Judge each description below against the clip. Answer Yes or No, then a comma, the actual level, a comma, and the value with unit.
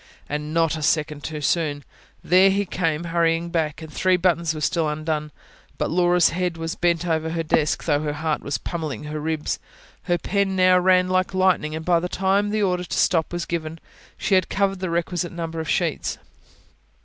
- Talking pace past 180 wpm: Yes, average, 195 wpm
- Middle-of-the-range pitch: Yes, medium, 170 Hz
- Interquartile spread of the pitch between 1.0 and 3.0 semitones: Yes, narrow, 2.6 semitones